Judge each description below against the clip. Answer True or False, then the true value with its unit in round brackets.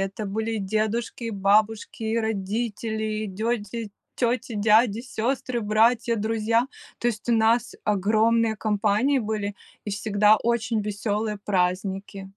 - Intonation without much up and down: True (1.9 semitones)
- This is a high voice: True (220 Hz)